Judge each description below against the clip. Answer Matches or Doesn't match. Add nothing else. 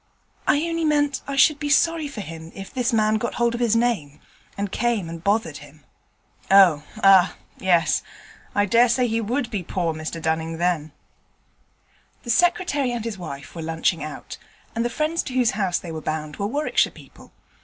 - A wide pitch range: Matches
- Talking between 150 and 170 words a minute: Doesn't match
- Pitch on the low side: Doesn't match